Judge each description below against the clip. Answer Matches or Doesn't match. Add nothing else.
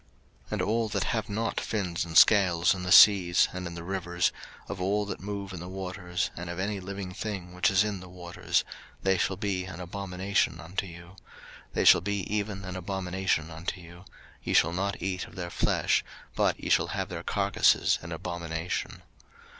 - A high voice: Doesn't match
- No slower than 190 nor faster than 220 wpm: Matches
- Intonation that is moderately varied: Doesn't match